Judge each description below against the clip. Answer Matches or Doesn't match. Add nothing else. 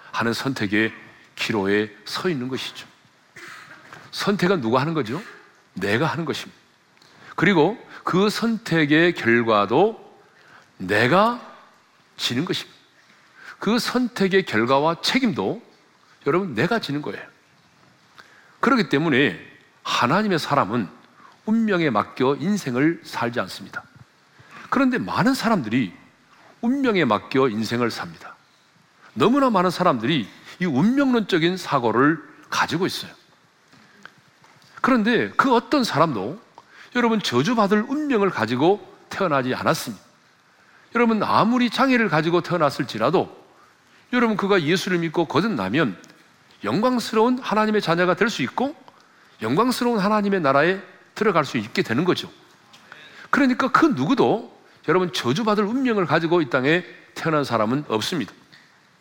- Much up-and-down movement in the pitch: Matches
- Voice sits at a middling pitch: Doesn't match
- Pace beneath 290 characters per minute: Matches